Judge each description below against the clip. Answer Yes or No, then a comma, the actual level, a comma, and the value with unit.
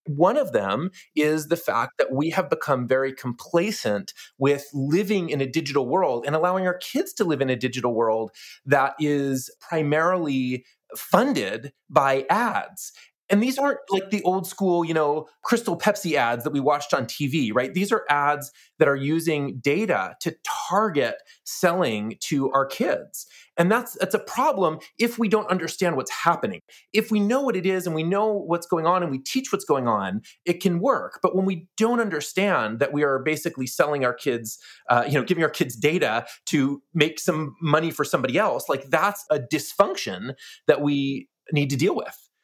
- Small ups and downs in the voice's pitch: No, wide, 5.4 semitones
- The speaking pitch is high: No, medium, 155 Hz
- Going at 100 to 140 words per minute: No, average, 190 wpm